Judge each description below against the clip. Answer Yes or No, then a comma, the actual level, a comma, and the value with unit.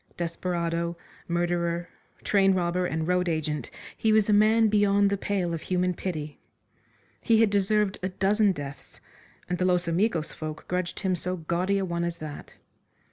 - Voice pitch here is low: No, medium, 180 Hz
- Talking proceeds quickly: No, average, 165 wpm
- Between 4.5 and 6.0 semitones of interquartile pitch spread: No, average, 2.7 semitones